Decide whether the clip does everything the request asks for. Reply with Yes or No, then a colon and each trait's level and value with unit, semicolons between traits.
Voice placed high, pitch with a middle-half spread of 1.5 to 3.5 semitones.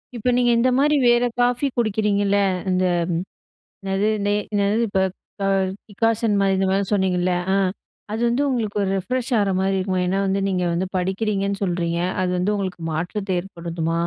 Yes: high, 195 Hz; average, 2.8 semitones